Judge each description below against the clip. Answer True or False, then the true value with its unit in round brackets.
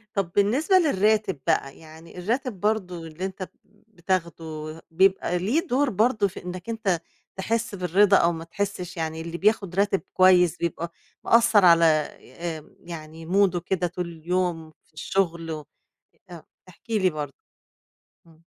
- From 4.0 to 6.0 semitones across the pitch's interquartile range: False (3.5 semitones)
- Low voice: False (180 Hz)